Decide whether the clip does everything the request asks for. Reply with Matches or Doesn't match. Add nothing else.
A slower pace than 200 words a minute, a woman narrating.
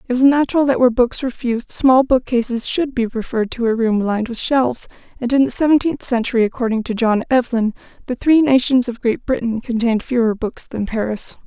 Doesn't match